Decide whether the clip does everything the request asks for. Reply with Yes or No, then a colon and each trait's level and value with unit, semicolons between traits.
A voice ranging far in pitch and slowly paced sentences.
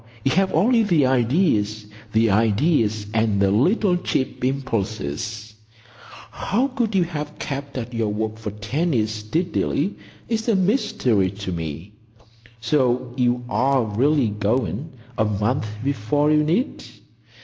Yes: wide, 6.2 semitones; slow, 125 wpm